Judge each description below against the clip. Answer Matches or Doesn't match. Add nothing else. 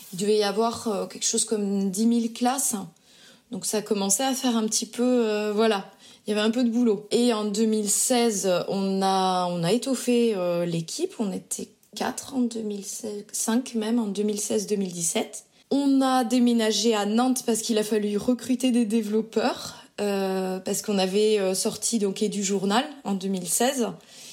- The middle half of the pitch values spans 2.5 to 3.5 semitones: Matches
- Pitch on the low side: Doesn't match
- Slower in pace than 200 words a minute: Matches